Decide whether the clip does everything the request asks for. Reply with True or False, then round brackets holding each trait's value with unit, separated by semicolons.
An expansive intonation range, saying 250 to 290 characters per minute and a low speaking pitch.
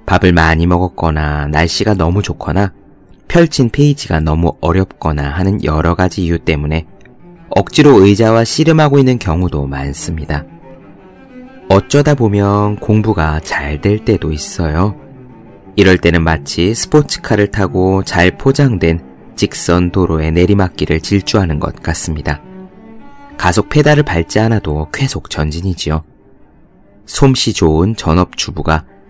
True (5.8 semitones; 280 characters per minute; 95 Hz)